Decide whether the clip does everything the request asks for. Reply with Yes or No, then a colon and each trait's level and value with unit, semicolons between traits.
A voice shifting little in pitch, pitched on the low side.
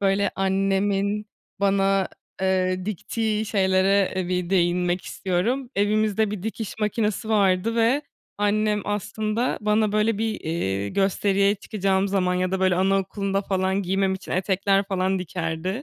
No: narrow, 2.0 semitones; high, 195 Hz